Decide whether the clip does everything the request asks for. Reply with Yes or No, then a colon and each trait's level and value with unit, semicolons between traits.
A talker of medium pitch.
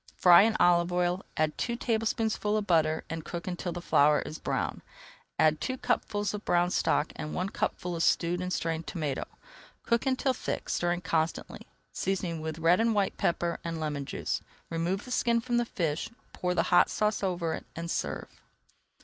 Yes: medium, 175 Hz